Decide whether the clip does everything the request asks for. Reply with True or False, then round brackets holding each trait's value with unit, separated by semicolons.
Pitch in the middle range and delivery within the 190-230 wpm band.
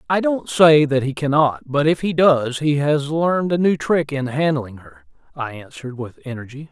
True (145 Hz; 205 wpm)